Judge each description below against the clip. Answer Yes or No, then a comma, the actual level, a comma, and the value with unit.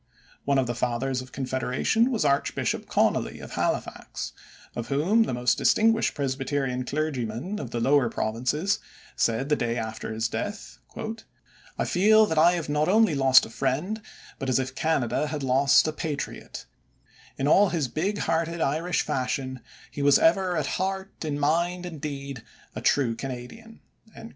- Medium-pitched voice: Yes, medium, 145 Hz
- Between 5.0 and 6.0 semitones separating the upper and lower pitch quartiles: Yes, average, 5.3 semitones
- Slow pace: No, average, 160 wpm